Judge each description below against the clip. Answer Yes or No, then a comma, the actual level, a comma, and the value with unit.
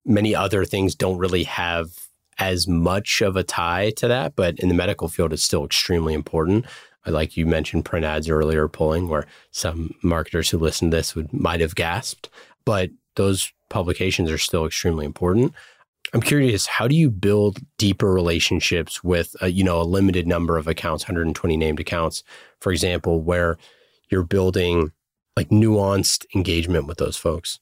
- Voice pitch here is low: Yes, very low, 90 Hz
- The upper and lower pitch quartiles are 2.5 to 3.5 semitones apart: Yes, average, 2.9 semitones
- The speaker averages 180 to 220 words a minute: No, average, 170 wpm